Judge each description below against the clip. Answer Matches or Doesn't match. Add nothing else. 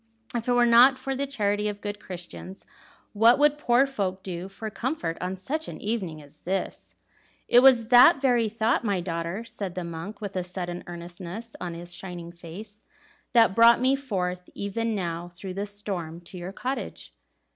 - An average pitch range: Matches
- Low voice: Doesn't match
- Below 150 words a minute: Doesn't match